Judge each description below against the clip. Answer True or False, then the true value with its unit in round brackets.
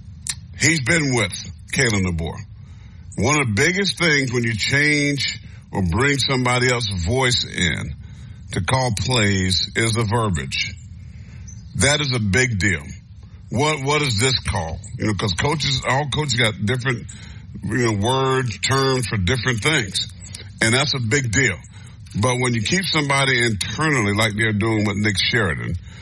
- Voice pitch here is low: True (110 Hz)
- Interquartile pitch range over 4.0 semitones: True (4.6 semitones)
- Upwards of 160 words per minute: False (155 wpm)